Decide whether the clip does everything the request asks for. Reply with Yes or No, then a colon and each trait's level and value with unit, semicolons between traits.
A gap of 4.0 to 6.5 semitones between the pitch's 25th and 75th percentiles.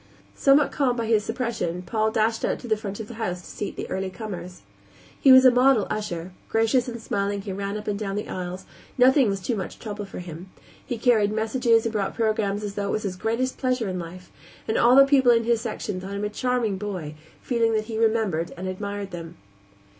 No: average, 3.2 semitones